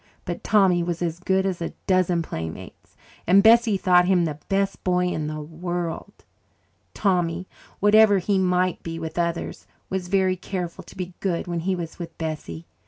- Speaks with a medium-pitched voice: Yes, medium, 180 Hz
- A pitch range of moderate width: No, narrow, 2.2 semitones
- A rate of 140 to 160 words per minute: No, average, 170 wpm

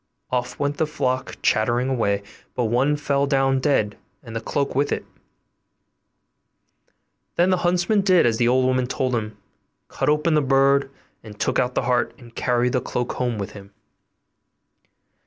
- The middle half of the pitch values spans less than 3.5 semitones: Yes, average, 3.0 semitones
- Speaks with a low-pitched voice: Yes, low, 130 Hz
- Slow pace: No, average, 160 wpm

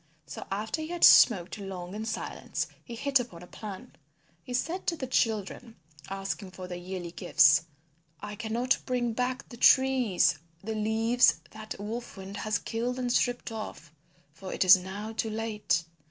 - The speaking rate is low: No, average, 175 wpm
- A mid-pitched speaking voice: No, high, 220 Hz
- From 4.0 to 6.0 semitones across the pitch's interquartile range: Yes, average, 4.4 semitones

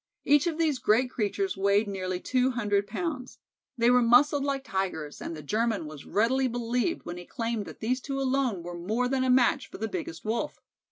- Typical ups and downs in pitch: Yes, average, 4.8 semitones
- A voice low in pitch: No, high, 235 Hz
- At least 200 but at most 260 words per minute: Yes, fast, 205 wpm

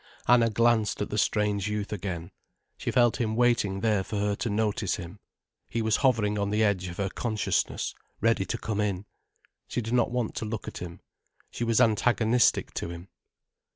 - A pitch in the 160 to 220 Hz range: No, low, 105 Hz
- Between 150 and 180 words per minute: No, average, 190 wpm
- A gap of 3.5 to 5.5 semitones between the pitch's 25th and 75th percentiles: No, narrow, 2.4 semitones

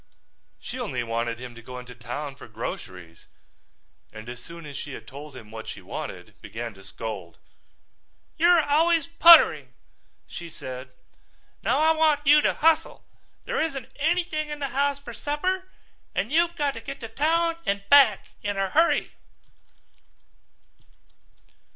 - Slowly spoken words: No, average, 150 wpm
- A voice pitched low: No, high, 225 Hz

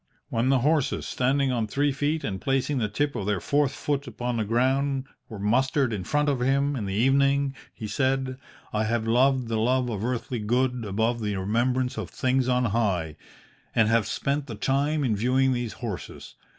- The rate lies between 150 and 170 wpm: No, average, 190 wpm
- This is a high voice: No, low, 125 Hz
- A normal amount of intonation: Yes, average, 3.4 semitones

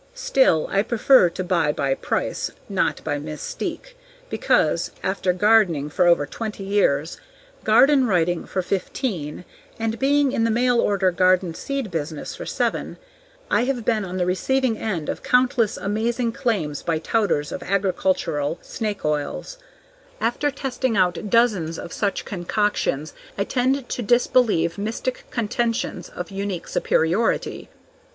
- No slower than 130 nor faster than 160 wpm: Yes, average, 140 wpm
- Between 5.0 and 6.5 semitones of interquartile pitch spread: Yes, wide, 5.6 semitones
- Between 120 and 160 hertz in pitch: No, high, 200 Hz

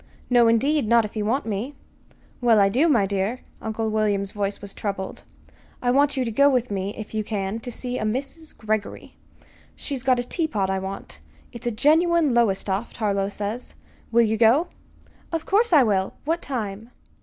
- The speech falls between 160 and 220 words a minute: Yes, average, 185 wpm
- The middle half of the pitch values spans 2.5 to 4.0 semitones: No, average, 4.4 semitones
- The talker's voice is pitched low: No, high, 225 Hz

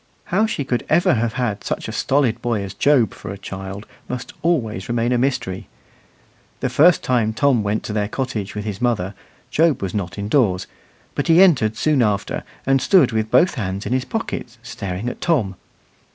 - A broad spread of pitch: No, average, 4.9 semitones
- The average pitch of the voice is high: No, low, 120 Hz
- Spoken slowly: No, average, 190 wpm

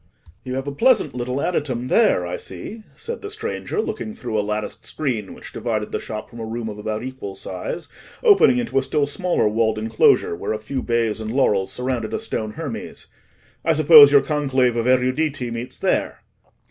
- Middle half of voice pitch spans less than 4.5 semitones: No, average, 5.3 semitones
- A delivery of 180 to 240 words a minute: Yes, average, 190 wpm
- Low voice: Yes, low, 125 Hz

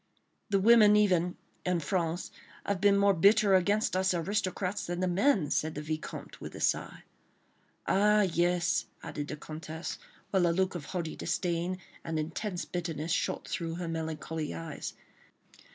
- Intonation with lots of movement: No, average, 3.4 semitones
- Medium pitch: Yes, medium, 175 Hz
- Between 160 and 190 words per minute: No, average, 150 wpm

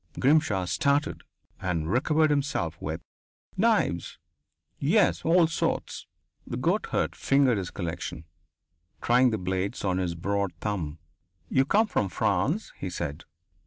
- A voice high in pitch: No, low, 100 Hz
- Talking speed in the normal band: No, slow, 125 wpm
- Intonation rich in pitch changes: Yes, wide, 8.3 semitones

